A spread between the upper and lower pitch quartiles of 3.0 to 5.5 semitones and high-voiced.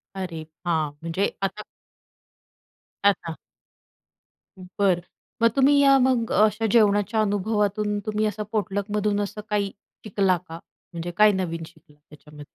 Yes: average, 3.4 semitones; high, 200 Hz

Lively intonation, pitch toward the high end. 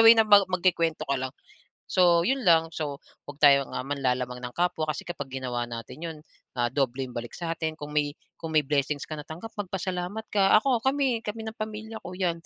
No: wide, 5.9 semitones; medium, 165 Hz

